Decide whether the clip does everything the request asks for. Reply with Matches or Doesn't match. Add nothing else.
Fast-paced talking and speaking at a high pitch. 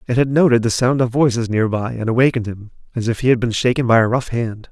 Doesn't match